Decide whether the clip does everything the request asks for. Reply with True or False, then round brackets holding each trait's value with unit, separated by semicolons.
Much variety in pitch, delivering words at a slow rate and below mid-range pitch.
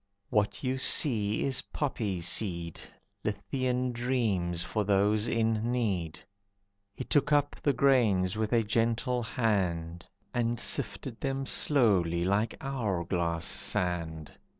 True (5.7 semitones; 120 wpm; 110 Hz)